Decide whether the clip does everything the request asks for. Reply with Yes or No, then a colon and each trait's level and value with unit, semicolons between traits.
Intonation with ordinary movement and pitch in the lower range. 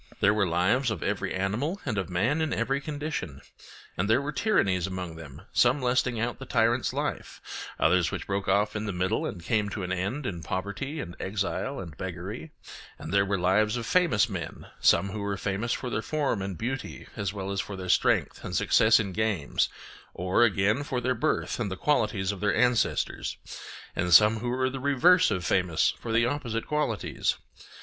Yes: average, 5.0 semitones; low, 105 Hz